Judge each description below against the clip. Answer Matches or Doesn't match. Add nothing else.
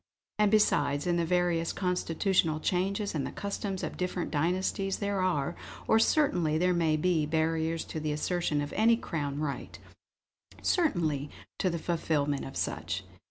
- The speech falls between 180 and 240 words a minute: Doesn't match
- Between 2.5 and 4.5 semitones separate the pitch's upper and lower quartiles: Matches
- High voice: Doesn't match